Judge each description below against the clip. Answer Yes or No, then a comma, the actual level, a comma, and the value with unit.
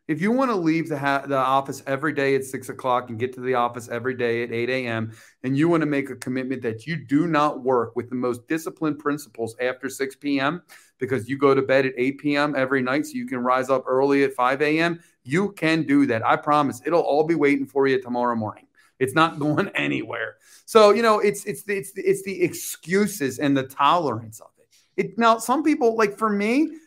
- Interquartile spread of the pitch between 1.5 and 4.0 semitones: No, average, 4.7 semitones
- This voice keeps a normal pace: No, fast, 230 wpm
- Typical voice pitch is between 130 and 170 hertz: Yes, medium, 140 Hz